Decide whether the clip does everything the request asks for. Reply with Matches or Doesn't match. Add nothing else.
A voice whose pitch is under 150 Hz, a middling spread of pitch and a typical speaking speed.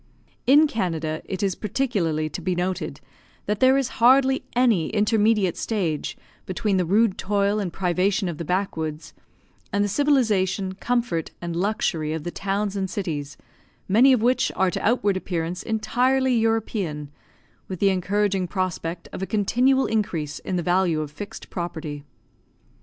Doesn't match